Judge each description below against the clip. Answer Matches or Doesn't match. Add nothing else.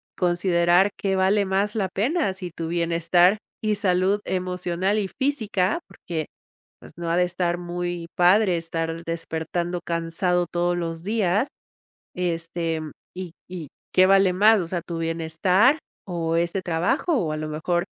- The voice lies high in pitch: Doesn't match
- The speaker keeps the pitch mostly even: Matches